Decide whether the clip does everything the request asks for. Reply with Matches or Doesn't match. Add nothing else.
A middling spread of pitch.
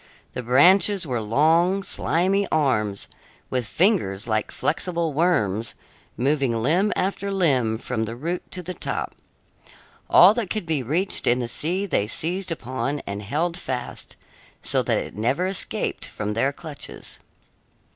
Doesn't match